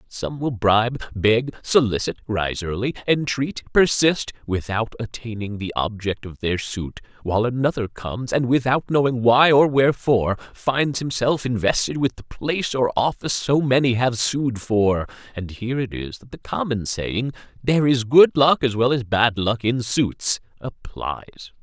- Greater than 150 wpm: Yes, average, 160 wpm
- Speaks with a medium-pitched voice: No, low, 120 Hz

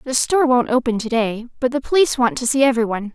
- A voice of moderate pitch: No, very high, 250 Hz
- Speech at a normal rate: No, fast, 265 wpm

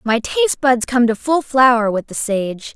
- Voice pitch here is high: Yes, high, 245 Hz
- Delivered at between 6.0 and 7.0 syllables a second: No, 5.0 syllables/s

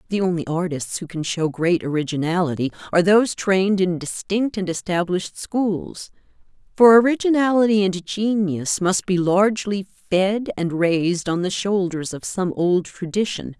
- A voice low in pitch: No, medium, 185 Hz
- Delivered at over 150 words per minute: No, average, 145 wpm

